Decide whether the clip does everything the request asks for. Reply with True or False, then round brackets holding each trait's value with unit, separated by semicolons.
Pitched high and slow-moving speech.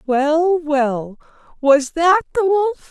True (310 Hz; 125 wpm)